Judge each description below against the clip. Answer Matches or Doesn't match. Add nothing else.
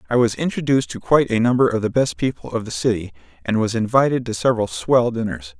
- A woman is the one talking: Doesn't match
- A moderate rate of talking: Doesn't match